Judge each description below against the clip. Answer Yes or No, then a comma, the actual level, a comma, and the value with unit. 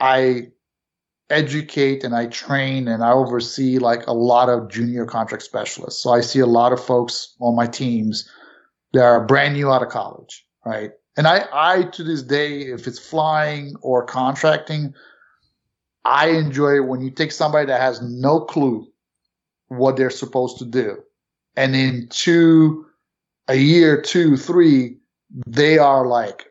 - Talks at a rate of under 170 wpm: Yes, average, 160 wpm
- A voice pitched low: Yes, low, 130 Hz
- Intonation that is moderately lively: Yes, average, 3.5 semitones